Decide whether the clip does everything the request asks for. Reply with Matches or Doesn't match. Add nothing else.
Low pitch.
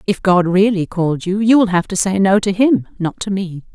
Doesn't match